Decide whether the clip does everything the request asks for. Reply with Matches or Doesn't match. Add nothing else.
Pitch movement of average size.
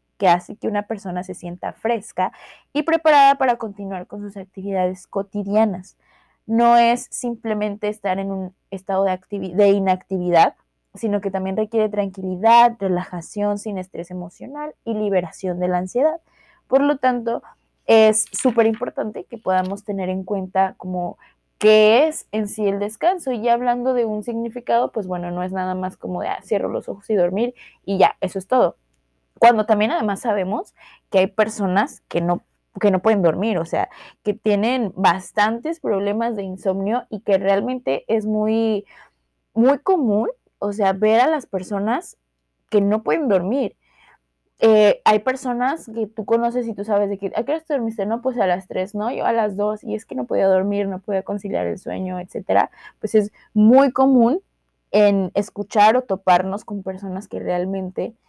Matches